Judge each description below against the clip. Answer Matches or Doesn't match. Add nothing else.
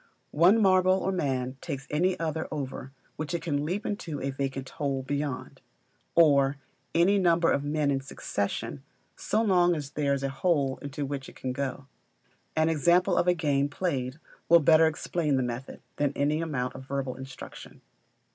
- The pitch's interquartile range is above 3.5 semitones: Matches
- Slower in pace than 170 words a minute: Doesn't match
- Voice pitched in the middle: Matches